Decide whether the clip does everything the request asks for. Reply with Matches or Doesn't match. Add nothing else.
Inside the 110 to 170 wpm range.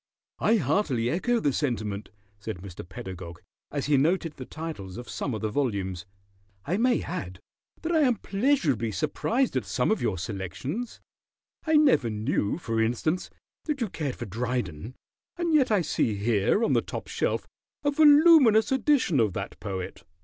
Matches